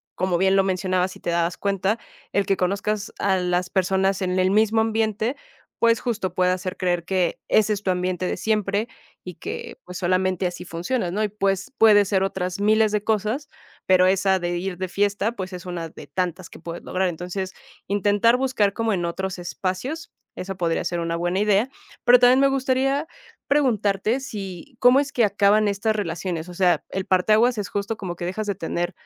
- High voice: Yes, high, 195 Hz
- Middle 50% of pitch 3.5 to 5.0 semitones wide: No, average, 3.0 semitones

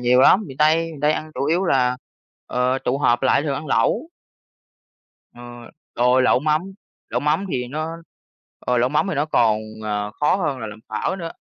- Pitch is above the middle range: No, low, 135 Hz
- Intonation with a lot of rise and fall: No, average, 3.8 semitones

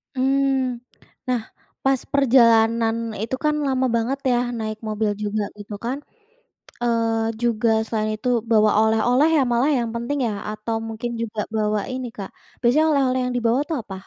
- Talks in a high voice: Yes, high, 235 Hz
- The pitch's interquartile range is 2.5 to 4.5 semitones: Yes, average, 2.9 semitones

